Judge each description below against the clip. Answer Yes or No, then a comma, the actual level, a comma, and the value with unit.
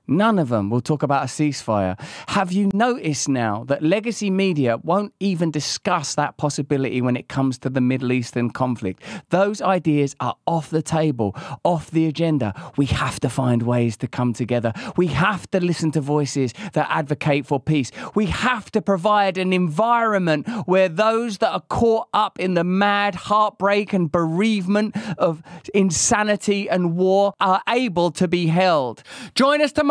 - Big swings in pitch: Yes, wide, 6.3 semitones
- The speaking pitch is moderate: Yes, medium, 175 Hz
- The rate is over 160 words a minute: Yes, average, 170 wpm